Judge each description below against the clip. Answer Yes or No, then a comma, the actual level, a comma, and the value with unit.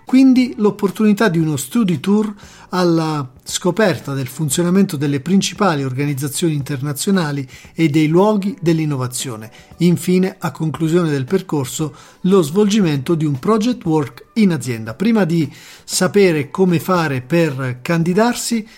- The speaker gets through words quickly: No, average, 120 wpm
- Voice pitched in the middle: Yes, medium, 170 Hz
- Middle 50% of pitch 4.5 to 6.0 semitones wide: Yes, average, 5.1 semitones